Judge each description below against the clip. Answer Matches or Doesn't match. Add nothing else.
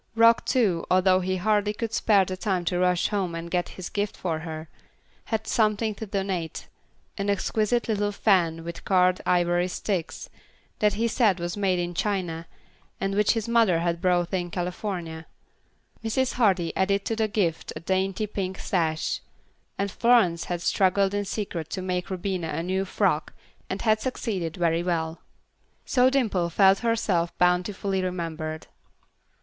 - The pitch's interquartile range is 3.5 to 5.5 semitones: Doesn't match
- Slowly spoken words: Doesn't match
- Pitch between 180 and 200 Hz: Matches